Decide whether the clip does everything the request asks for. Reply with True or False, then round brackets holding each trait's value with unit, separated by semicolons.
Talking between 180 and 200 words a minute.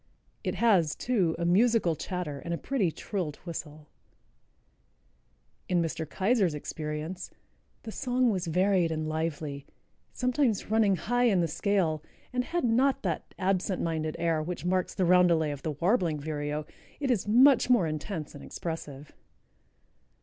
False (145 wpm)